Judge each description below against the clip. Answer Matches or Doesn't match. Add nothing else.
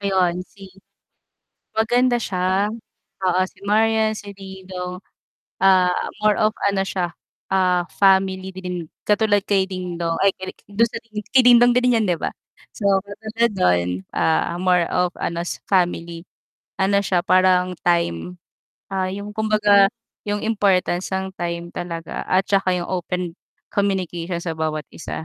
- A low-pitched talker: Doesn't match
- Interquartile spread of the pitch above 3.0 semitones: Doesn't match